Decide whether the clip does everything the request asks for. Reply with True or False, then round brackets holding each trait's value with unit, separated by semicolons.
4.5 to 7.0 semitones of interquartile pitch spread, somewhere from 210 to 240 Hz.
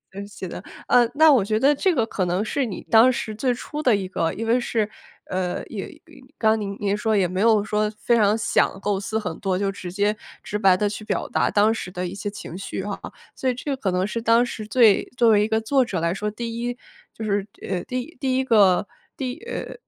False (3.2 semitones; 215 Hz)